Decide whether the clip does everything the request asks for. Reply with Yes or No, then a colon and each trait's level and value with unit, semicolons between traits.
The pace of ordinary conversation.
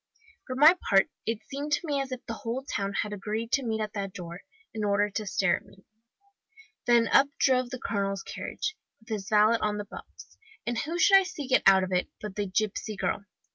No: fast, 220 wpm